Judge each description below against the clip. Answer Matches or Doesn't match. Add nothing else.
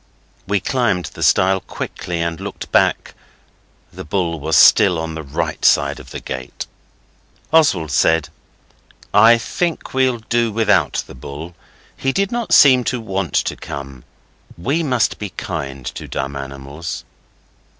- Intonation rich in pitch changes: Matches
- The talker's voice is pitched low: Matches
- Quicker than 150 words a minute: Doesn't match